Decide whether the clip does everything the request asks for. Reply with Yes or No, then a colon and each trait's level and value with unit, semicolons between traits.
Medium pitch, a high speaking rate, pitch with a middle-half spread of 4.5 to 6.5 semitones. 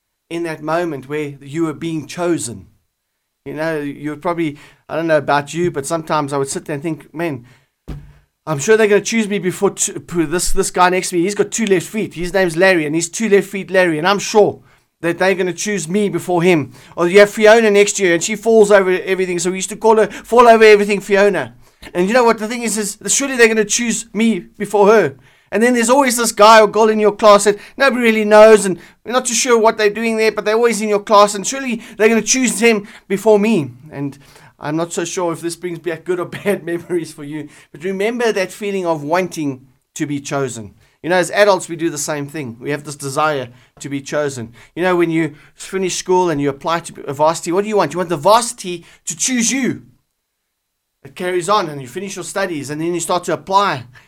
Yes: medium, 180 Hz; fast, 245 wpm; average, 5.2 semitones